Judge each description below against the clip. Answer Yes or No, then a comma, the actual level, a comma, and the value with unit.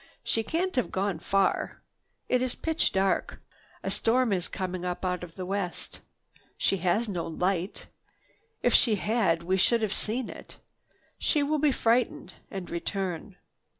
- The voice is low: No, high, 195 Hz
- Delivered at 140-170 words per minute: Yes, average, 155 wpm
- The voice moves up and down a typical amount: Yes, average, 4.6 semitones